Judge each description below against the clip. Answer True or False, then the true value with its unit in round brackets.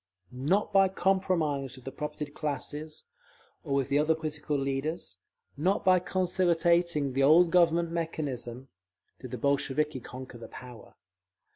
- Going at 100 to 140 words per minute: True (135 wpm)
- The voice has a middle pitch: True (150 Hz)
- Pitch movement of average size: True (3.9 semitones)